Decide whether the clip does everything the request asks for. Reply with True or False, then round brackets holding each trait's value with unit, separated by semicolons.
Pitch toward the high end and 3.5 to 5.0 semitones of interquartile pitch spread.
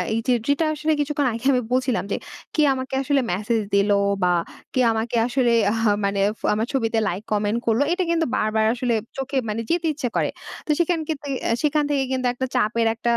True (250 Hz; 4.2 semitones)